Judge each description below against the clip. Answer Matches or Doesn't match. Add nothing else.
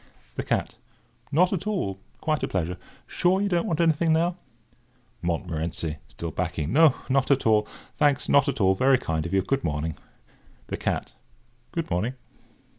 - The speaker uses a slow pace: Doesn't match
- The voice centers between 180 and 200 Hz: Doesn't match